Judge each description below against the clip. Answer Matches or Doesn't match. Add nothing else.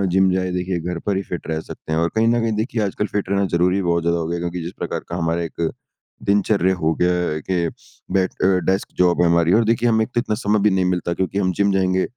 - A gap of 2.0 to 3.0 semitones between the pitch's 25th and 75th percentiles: Matches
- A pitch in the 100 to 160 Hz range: Doesn't match